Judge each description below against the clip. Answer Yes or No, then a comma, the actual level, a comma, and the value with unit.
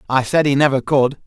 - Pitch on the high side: No, low, 135 Hz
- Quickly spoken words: Yes, fast, 240 wpm